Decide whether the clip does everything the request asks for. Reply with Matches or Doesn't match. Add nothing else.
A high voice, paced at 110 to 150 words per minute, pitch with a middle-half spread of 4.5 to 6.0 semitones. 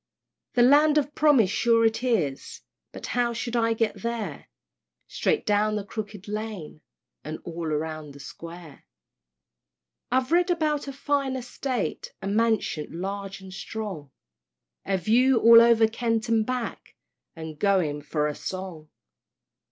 Matches